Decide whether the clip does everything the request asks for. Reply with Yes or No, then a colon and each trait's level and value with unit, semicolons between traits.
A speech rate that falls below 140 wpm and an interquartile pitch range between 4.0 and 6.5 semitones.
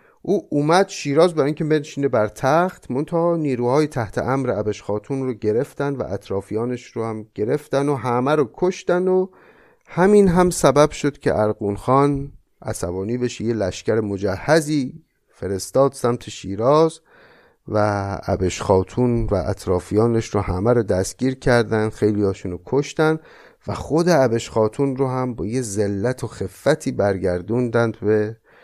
No: average, 145 wpm; wide, 5.6 semitones